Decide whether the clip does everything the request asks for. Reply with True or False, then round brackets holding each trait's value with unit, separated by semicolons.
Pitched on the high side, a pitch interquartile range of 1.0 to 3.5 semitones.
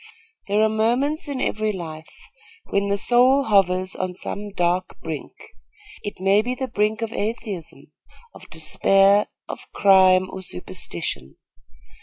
True (200 Hz; 3.1 semitones)